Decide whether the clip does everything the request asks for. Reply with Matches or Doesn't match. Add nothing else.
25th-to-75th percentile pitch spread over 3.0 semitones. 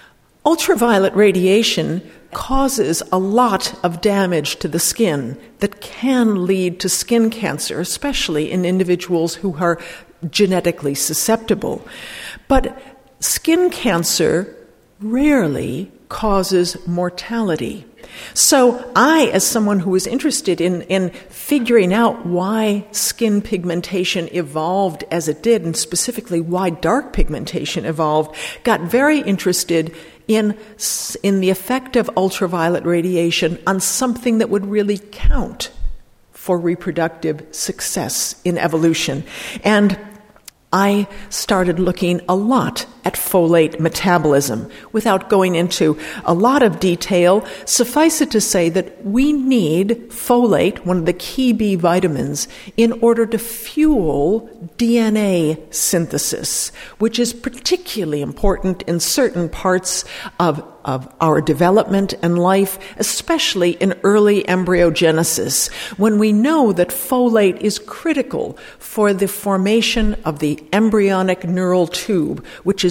Matches